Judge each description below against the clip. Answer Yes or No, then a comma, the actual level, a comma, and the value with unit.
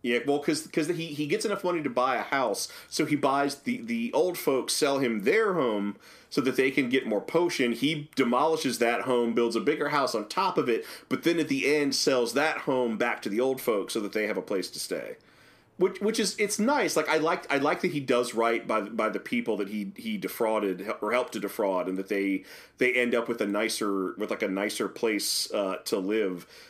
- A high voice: No, medium, 140 Hz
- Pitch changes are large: Yes, wide, 6.0 semitones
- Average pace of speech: No, fast, 240 wpm